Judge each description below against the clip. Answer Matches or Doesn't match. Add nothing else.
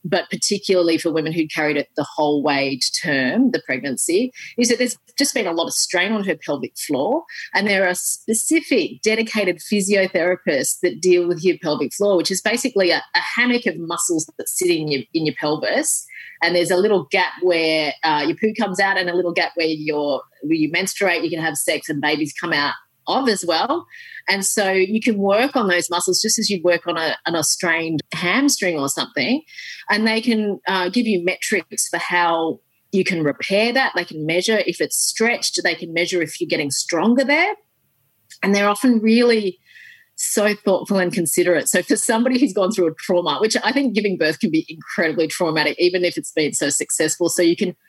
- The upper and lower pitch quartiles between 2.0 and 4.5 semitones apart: Doesn't match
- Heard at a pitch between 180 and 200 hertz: Matches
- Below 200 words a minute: Doesn't match